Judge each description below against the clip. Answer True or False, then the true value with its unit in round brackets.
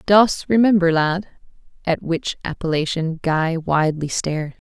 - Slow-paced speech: True (115 wpm)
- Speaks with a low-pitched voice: False (170 Hz)